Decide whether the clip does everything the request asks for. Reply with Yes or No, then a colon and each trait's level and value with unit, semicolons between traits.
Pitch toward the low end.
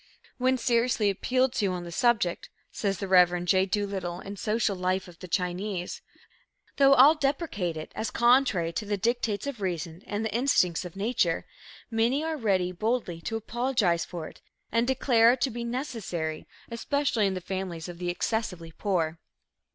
No: high, 205 Hz